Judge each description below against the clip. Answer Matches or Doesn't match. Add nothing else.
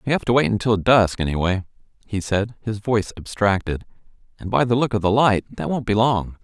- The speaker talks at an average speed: Doesn't match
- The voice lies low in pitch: Matches